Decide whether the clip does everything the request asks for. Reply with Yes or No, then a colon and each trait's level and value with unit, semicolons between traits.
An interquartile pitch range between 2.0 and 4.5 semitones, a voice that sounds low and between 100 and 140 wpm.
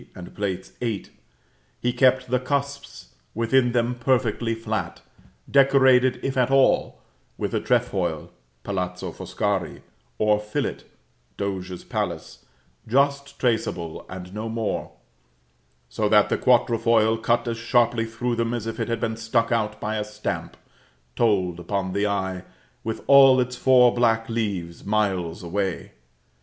Yes: average, 3.4 semitones; low, 115 Hz; slow, 135 wpm